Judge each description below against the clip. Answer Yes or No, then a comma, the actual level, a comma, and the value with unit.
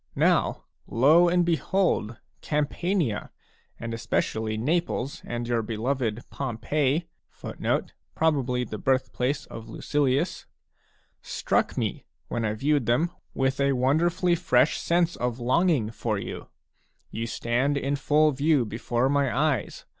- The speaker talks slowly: Yes, slow, 110 wpm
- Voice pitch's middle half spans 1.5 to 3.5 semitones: No, average, 4.5 semitones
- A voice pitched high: No, low, 135 Hz